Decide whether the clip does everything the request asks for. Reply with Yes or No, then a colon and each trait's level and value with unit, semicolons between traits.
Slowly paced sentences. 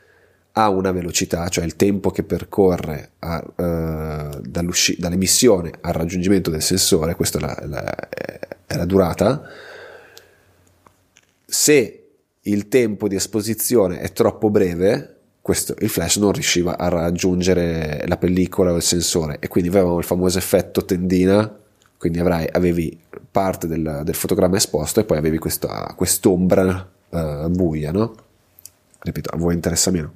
No: average, 140 wpm